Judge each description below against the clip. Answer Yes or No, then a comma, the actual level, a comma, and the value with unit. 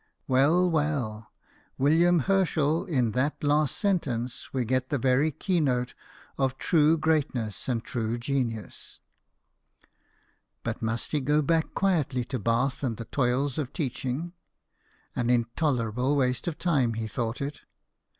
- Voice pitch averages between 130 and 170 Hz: Yes, low, 135 Hz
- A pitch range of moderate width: Yes, average, 4.1 semitones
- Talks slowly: Yes, slow, 130 wpm